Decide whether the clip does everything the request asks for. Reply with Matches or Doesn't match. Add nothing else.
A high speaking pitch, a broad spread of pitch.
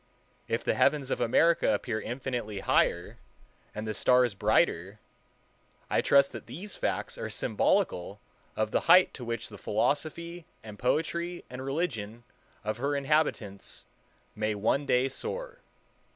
Doesn't match